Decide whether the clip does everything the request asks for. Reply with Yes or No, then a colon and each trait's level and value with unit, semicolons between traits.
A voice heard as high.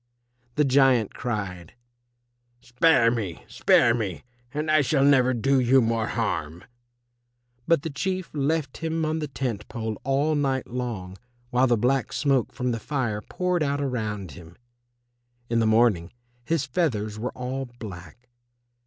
No: low, 125 Hz